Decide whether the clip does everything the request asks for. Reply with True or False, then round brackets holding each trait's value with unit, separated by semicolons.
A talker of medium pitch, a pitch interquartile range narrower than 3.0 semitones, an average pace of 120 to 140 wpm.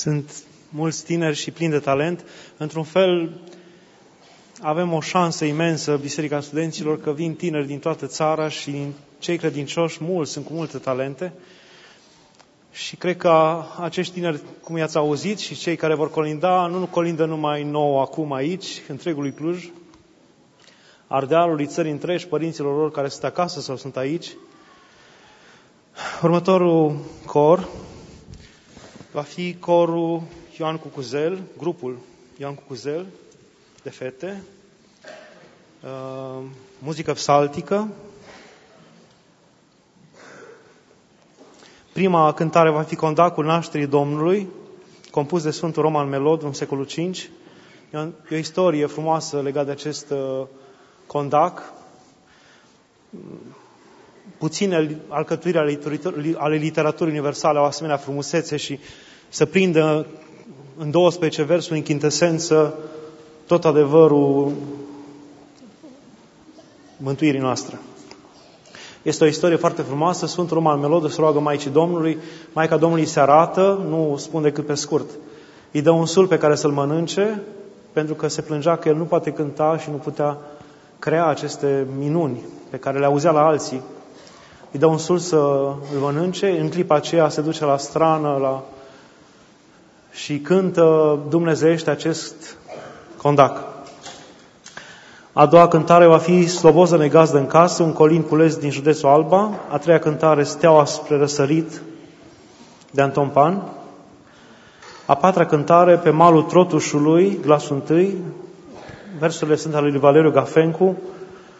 True (155 Hz; 2.6 semitones; 125 wpm)